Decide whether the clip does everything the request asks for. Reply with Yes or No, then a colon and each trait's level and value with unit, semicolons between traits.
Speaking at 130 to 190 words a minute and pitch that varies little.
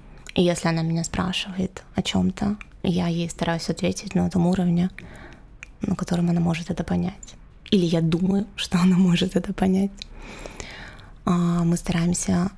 Yes: average, 150 wpm; narrow, 1.5 semitones